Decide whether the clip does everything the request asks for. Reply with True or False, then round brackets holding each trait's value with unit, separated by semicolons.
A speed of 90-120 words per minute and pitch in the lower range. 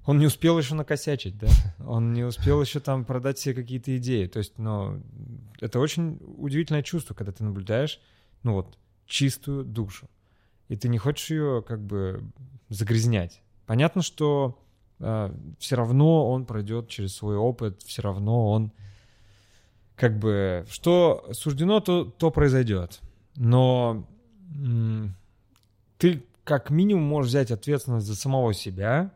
False (140 wpm; 120 Hz)